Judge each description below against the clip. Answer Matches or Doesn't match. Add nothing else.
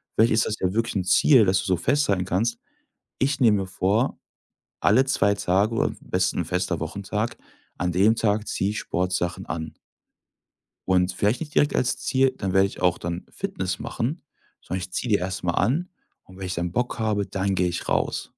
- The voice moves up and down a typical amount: Matches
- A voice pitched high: Doesn't match